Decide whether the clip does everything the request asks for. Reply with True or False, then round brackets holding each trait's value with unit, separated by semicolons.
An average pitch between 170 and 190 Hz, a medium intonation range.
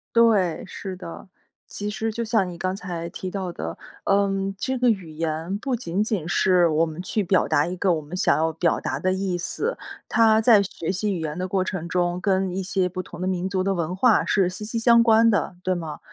True (185 Hz; 3.0 semitones)